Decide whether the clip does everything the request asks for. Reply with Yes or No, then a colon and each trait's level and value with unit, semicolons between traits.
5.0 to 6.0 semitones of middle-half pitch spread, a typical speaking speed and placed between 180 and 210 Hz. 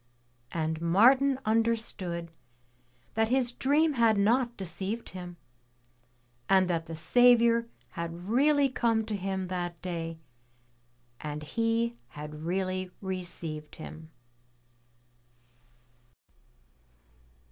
No: wide, 5.6 semitones; slow, 90 wpm; high, 190 Hz